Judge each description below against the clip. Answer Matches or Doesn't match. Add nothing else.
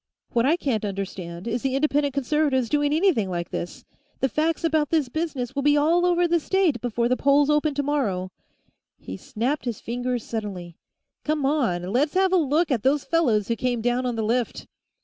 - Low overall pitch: Doesn't match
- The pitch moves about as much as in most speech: Matches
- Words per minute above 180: Matches